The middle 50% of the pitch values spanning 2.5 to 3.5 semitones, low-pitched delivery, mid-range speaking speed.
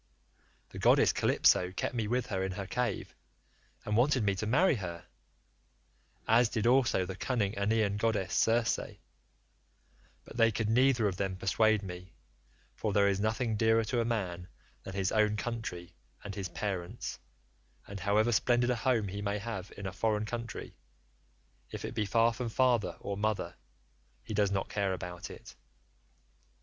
Yes: average, 3.1 semitones; low, 105 Hz; average, 165 wpm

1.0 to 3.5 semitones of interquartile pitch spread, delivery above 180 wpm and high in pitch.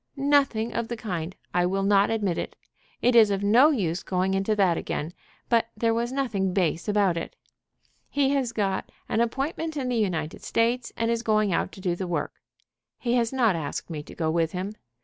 No: average, 4.5 semitones; fast, 205 wpm; high, 210 Hz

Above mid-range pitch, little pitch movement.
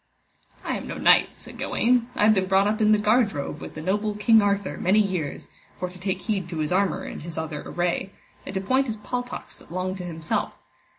No: high, 195 Hz; average, 3.2 semitones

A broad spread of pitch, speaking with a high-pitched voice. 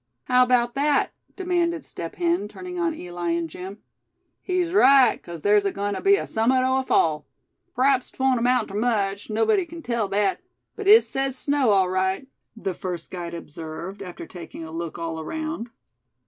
Yes: wide, 7.2 semitones; high, 225 Hz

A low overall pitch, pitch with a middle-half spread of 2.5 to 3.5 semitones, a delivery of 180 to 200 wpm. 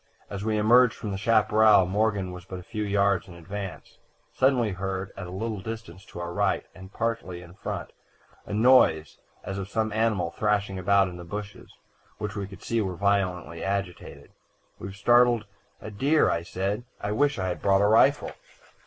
Yes: low, 100 Hz; average, 2.8 semitones; average, 185 wpm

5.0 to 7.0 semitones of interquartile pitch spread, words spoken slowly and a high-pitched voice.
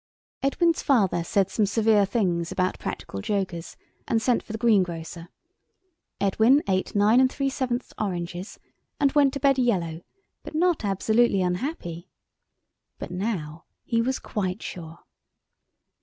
Yes: wide, 5.6 semitones; slow, 125 wpm; high, 205 Hz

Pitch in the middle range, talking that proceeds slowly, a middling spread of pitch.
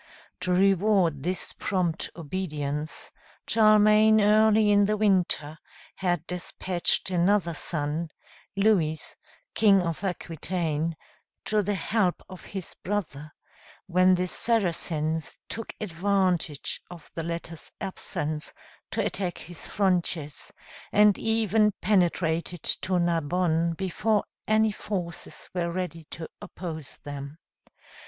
Yes: medium, 180 Hz; slow, 105 wpm; average, 3.7 semitones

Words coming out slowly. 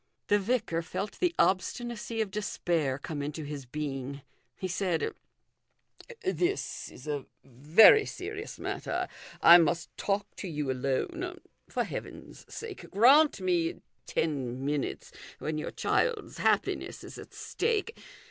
Yes: slow, 130 wpm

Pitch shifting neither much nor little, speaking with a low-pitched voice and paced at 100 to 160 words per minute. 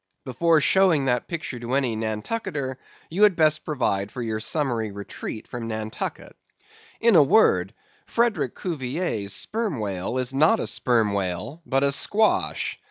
No: wide, 7.2 semitones; low, 130 Hz; average, 150 wpm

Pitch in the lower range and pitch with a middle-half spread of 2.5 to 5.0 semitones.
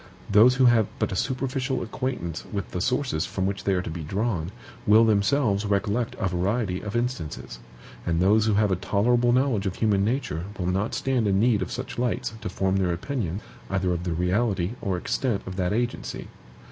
Yes: low, 100 Hz; average, 4.6 semitones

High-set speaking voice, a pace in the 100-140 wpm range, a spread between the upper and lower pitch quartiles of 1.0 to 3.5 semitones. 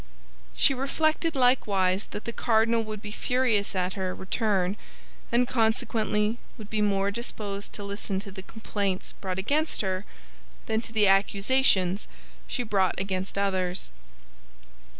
Yes: high, 210 Hz; slow, 135 wpm; average, 3.1 semitones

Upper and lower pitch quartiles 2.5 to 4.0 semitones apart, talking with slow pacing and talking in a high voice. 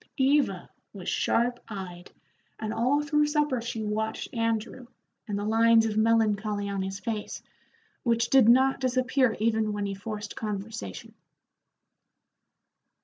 Yes: average, 2.9 semitones; slow, 130 wpm; high, 225 Hz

